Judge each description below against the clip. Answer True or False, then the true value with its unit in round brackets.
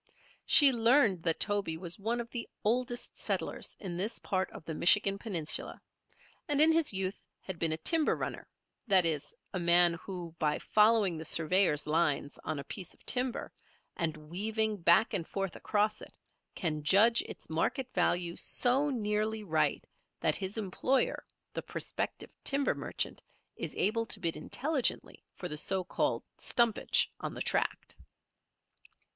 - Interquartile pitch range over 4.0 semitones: True (5.3 semitones)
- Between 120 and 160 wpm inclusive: True (155 wpm)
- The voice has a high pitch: True (195 Hz)